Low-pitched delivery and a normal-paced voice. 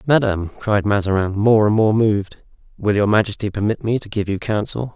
Yes: low, 105 Hz; average, 195 wpm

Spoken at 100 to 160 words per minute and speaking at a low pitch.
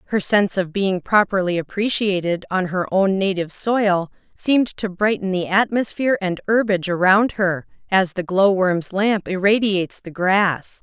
No: average, 150 wpm; high, 190 Hz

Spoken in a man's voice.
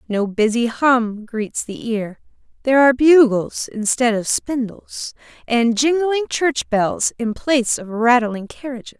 No: female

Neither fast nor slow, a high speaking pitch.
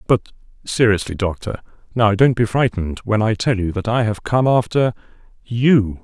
No: average, 150 wpm; low, 110 Hz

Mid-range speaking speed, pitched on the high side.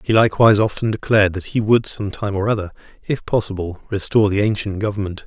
No: average, 195 wpm; low, 105 Hz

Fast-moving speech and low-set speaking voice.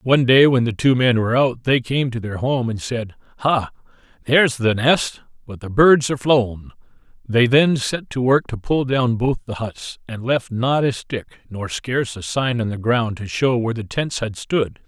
Yes: fast, 220 wpm; low, 120 Hz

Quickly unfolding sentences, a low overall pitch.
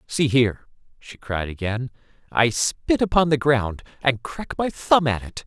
No: average, 165 wpm; low, 130 Hz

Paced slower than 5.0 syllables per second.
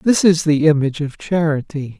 No: 5.1 syllables/s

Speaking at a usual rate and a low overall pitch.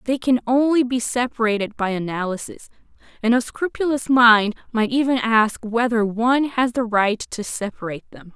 No: average, 160 wpm; high, 235 Hz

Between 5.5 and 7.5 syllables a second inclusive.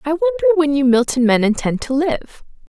Yes: 5.9 syllables/s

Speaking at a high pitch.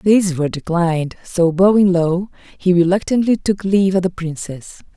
No: medium, 180 Hz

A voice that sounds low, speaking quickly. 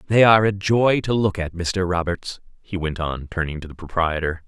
Yes: very low, 90 Hz; fast, 215 wpm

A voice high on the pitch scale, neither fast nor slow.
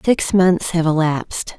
No: medium, 170 Hz; average, 150 wpm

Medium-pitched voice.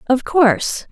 No: very high, 280 Hz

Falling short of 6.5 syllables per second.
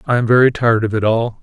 No: 6.9 syllables/s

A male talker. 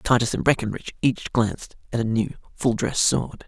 Yes: male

